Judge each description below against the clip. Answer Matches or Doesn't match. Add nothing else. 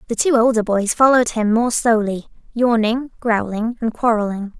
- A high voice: Matches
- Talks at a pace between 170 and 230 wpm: Doesn't match